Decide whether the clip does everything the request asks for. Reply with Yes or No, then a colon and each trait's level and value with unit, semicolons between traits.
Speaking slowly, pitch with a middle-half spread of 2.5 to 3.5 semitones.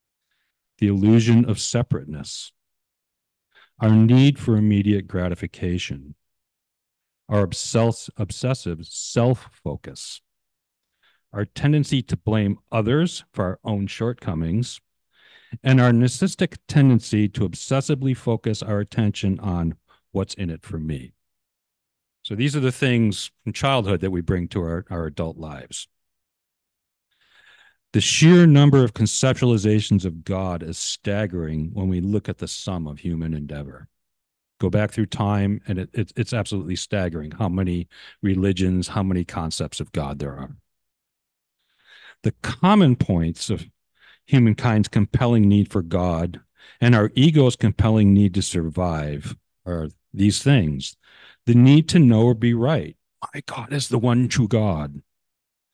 No: slow, 130 wpm; wide, 5.5 semitones